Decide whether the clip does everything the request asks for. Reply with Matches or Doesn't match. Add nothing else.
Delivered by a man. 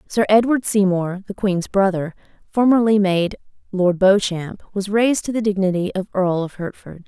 Doesn't match